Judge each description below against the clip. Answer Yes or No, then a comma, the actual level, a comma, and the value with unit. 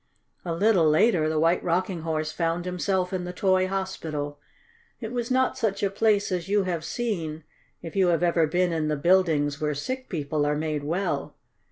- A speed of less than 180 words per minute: No, average, 190 wpm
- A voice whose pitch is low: No, medium, 175 Hz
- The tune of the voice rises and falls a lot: No, average, 3.7 semitones